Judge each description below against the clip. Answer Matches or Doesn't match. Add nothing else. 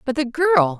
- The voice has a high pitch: Matches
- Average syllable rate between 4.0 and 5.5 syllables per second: Matches